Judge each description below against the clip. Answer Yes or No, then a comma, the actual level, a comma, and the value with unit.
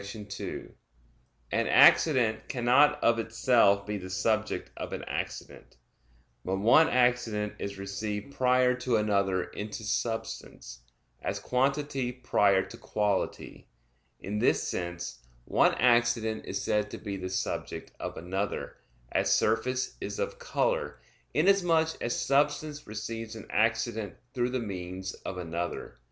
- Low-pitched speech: Yes, low, 110 Hz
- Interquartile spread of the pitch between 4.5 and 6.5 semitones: No, average, 4.1 semitones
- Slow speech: Yes, slow, 130 wpm